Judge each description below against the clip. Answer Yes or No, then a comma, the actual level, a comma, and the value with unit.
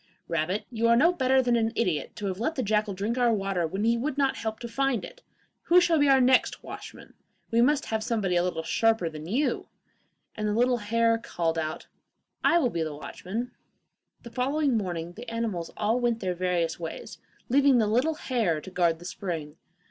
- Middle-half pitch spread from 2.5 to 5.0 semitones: No, wide, 5.6 semitones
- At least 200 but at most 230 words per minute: Yes, fast, 205 wpm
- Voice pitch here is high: Yes, high, 225 Hz